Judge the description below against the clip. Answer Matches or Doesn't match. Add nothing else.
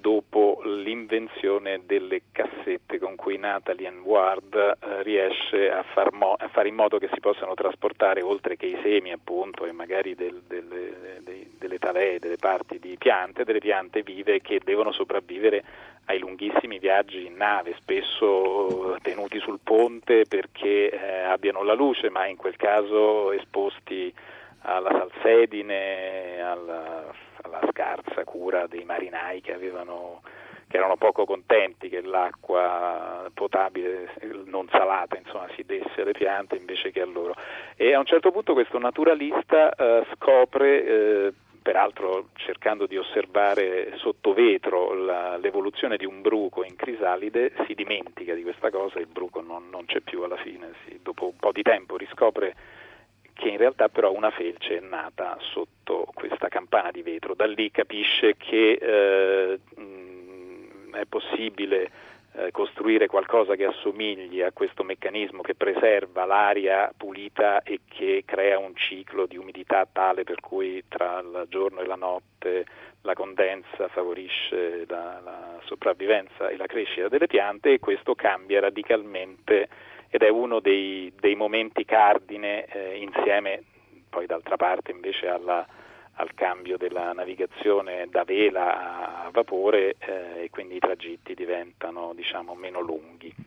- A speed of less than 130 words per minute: Doesn't match